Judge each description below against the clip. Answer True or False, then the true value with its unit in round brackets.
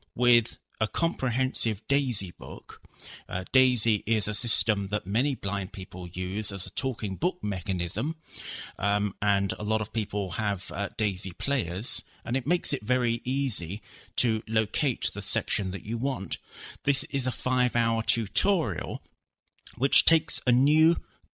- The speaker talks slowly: False (150 wpm)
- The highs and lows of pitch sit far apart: False (4.4 semitones)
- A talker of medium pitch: False (110 Hz)